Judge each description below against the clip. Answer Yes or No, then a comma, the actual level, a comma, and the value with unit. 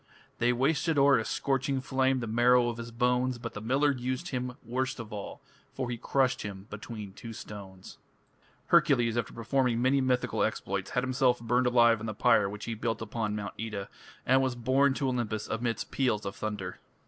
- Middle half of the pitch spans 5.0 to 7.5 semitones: No, average, 3.1 semitones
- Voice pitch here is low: Yes, low, 120 Hz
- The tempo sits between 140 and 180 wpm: No, average, 190 wpm